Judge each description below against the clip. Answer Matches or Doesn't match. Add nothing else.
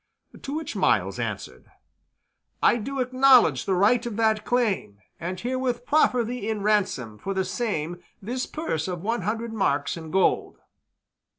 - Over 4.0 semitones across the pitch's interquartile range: Matches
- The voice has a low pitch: Doesn't match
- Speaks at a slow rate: Doesn't match